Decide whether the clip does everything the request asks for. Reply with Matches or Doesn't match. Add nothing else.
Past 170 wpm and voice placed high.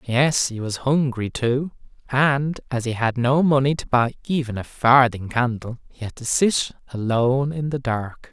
Doesn't match